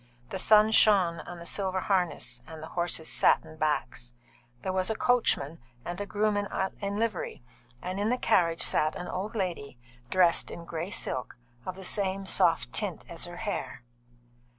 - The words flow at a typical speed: Yes, average, 170 wpm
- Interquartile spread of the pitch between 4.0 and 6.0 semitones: No, average, 3.6 semitones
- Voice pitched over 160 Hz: Yes, medium, 185 Hz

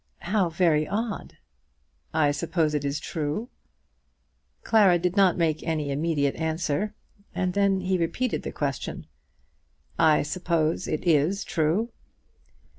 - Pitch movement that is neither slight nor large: Yes, average, 3.6 semitones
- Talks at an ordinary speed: No, slow, 120 wpm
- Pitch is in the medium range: Yes, medium, 170 Hz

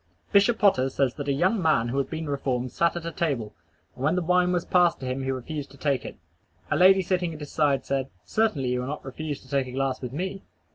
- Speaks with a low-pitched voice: No, medium, 145 Hz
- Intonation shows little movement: No, average, 4.9 semitones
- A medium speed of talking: No, fast, 250 wpm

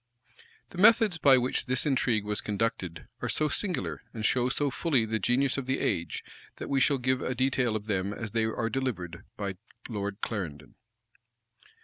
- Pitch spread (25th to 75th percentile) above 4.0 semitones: Yes, average, 4.7 semitones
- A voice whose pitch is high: No, low, 120 Hz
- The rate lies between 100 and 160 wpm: No, average, 175 wpm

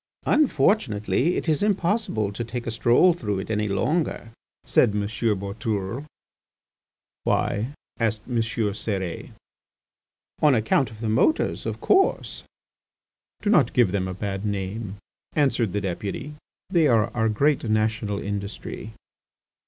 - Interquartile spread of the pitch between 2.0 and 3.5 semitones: No, average, 4.8 semitones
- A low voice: Yes, low, 110 Hz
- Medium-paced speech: No, slow, 130 wpm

